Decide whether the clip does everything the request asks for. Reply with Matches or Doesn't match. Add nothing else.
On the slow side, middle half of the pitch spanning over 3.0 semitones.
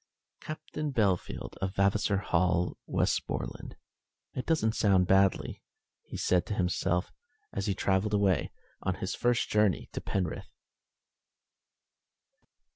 Doesn't match